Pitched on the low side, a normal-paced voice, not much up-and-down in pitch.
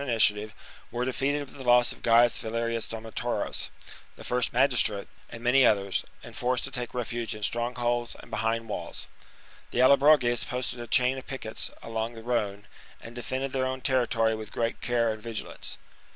Yes: low, 120 Hz; average, 180 wpm; narrow, 1.9 semitones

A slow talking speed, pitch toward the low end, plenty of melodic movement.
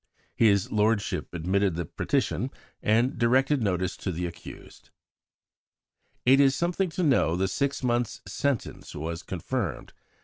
Yes: slow, 130 wpm; low, 110 Hz; wide, 6.5 semitones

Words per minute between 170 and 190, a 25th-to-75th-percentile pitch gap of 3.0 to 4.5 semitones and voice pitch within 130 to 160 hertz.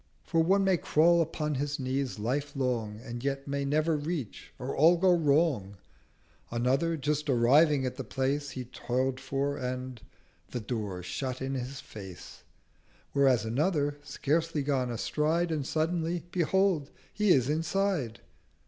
No: average, 145 wpm; average, 4.1 semitones; medium, 140 Hz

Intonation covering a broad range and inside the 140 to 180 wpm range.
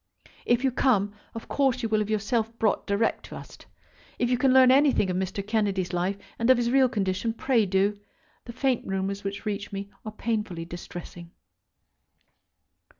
No: average, 3.6 semitones; average, 175 wpm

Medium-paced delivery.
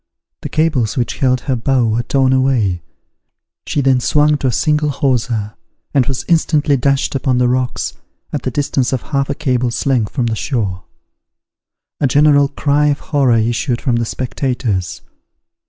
Yes: average, 165 wpm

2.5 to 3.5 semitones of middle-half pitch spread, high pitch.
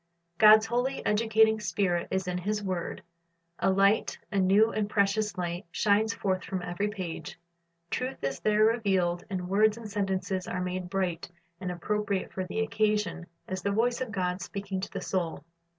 Yes: average, 2.8 semitones; high, 195 Hz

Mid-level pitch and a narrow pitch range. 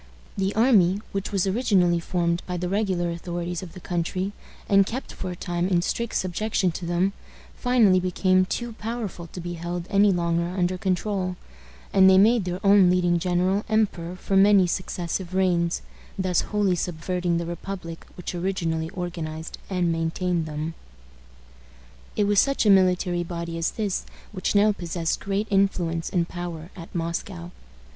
Yes: medium, 180 Hz; narrow, 2.3 semitones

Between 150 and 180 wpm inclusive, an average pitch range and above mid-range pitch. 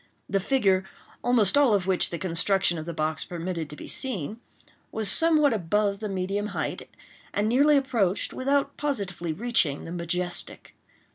No: average, 155 wpm; wide, 5.7 semitones; high, 200 Hz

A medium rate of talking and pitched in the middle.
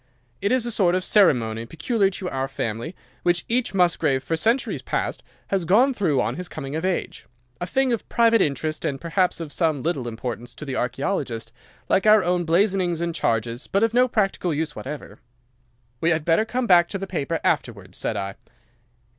Yes: average, 190 wpm; medium, 170 Hz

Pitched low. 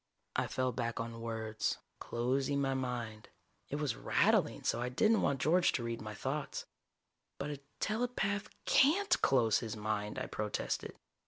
Yes: low, 125 Hz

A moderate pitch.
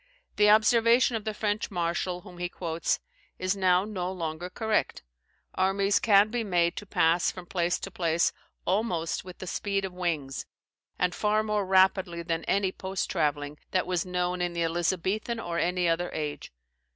Yes: medium, 180 Hz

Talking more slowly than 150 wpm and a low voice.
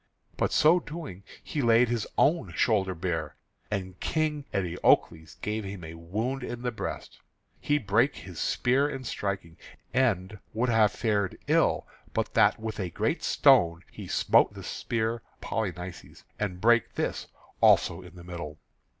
No: average, 155 wpm; low, 105 Hz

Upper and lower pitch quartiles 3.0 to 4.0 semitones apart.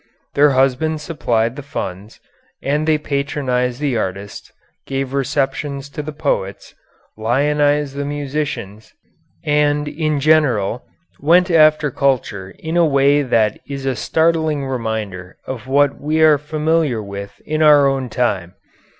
Yes: average, 3.5 semitones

